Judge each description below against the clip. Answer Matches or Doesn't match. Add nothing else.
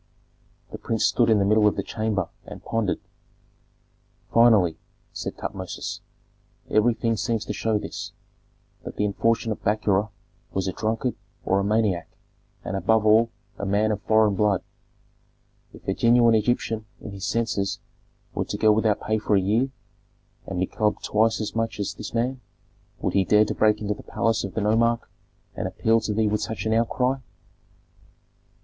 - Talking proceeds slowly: Doesn't match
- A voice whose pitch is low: Matches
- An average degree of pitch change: Doesn't match